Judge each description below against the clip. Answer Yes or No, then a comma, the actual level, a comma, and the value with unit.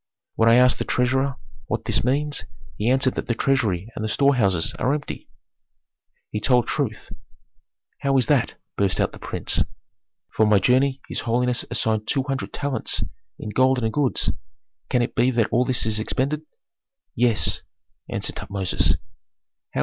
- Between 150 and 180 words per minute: Yes, average, 155 wpm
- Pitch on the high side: No, low, 125 Hz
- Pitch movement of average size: Yes, average, 3.5 semitones